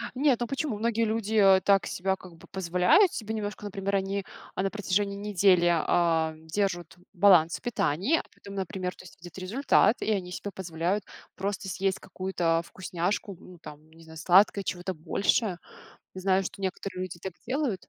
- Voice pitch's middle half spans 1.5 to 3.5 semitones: Yes, average, 2.7 semitones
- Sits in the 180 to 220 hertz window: Yes, high, 190 Hz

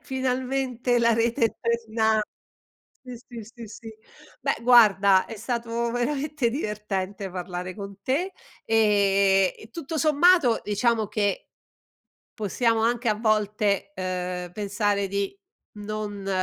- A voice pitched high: Yes, high, 220 Hz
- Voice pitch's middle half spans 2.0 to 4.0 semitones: Yes, average, 3.3 semitones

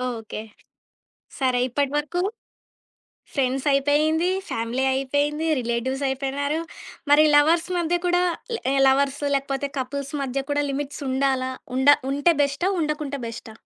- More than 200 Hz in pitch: Yes, very high, 275 Hz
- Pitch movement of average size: No, narrow, 2.0 semitones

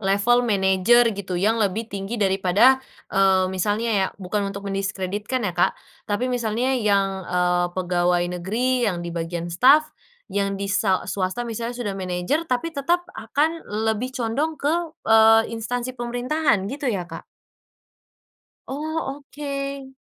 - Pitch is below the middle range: No, high, 215 Hz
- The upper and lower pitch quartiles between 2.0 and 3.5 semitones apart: No, average, 4.8 semitones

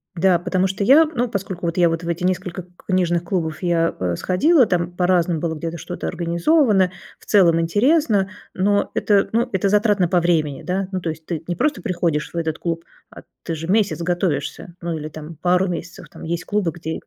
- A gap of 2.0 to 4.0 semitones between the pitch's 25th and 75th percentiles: Yes, narrow, 2.6 semitones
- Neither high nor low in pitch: Yes, medium, 175 Hz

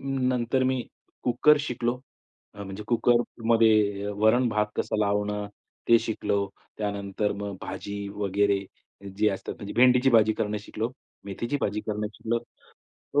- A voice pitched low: Yes, low, 105 Hz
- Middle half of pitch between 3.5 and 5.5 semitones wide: No, average, 2.8 semitones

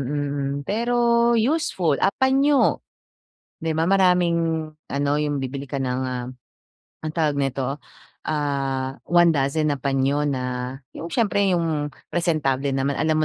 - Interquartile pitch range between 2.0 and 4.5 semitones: Yes, average, 3.7 semitones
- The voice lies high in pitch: No, medium, 145 Hz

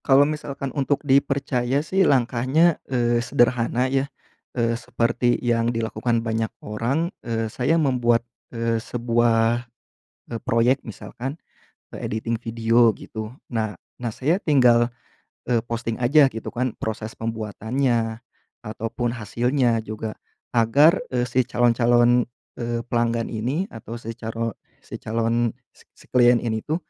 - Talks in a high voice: No, low, 120 Hz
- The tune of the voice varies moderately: No, narrow, 2.0 semitones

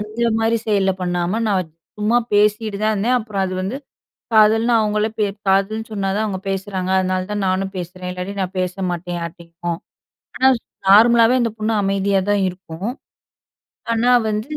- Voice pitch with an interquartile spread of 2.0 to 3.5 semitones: Yes, average, 2.8 semitones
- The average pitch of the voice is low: No, high, 200 Hz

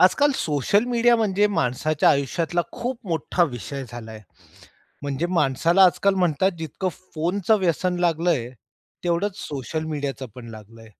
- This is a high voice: No, medium, 165 Hz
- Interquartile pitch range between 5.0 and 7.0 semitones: Yes, wide, 5.5 semitones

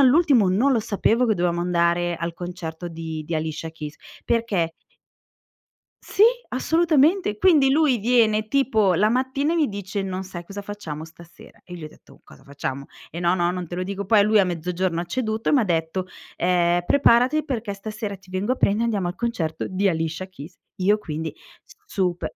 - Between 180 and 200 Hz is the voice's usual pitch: Yes, high, 190 Hz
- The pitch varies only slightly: No, average, 5.1 semitones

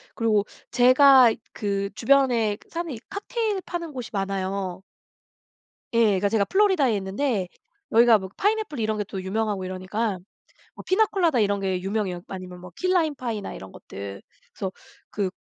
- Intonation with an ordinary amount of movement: No, wide, 6.3 semitones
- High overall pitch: Yes, high, 215 Hz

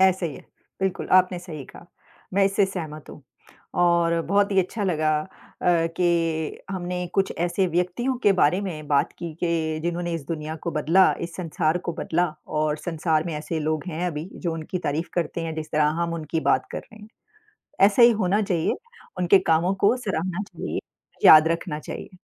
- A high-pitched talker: No, medium, 170 Hz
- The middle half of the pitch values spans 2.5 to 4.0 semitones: Yes, average, 2.8 semitones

